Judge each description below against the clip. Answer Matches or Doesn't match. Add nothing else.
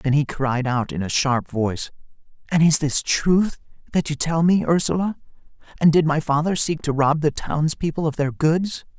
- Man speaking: Matches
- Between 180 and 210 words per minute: Matches